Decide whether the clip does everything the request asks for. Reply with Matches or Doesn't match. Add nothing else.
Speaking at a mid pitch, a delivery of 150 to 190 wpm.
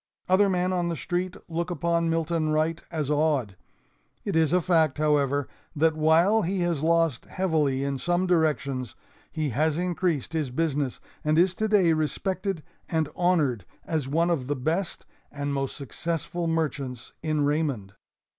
Matches